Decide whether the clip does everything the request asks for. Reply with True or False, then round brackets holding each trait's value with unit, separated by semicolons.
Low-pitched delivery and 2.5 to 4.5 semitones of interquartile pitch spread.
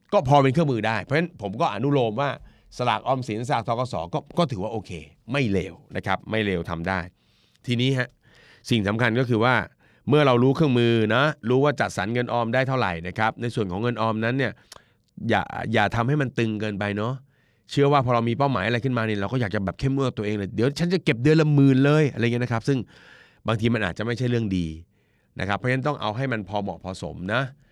True (120 Hz; 4.1 semitones)